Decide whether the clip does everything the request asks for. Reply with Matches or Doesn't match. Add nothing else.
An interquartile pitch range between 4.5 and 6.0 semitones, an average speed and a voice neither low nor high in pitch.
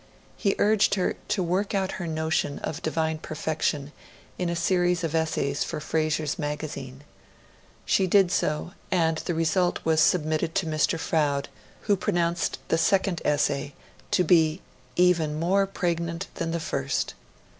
Doesn't match